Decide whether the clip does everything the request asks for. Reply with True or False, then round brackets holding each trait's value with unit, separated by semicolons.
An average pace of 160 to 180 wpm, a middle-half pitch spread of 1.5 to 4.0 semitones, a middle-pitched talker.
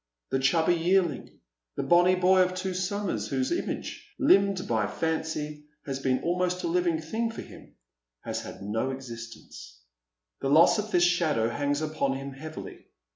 False (165 wpm; 5.1 semitones; 160 Hz)